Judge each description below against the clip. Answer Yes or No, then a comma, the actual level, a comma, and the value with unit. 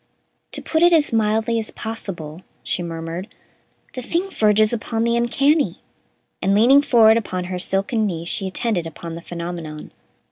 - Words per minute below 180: Yes, average, 155 wpm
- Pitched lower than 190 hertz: No, high, 215 Hz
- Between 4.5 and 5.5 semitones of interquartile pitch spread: Yes, average, 5.1 semitones